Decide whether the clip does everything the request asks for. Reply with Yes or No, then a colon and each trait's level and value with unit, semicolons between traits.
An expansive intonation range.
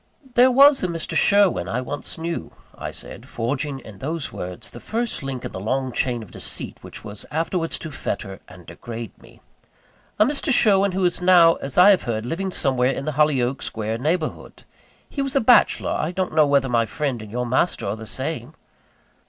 Yes: wide, 7.3 semitones